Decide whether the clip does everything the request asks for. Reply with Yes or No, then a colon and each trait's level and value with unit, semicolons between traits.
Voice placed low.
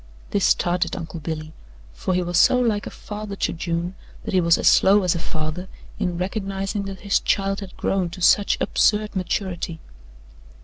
No: medium, 185 Hz